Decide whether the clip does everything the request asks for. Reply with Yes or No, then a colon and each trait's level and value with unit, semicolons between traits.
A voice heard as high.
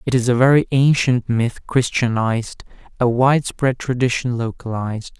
No: low, 120 Hz